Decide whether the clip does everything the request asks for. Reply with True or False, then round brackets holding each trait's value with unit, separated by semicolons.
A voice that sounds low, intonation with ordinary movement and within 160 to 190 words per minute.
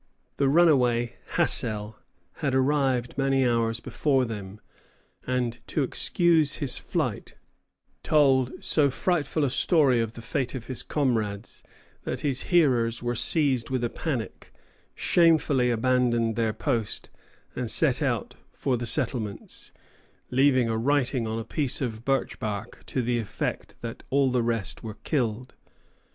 False (125 Hz; 3.3 semitones; 140 wpm)